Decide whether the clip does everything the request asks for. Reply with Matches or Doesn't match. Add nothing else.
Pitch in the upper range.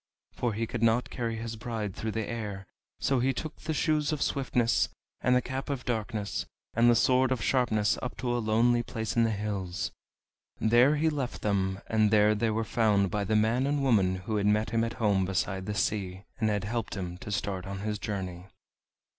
Doesn't match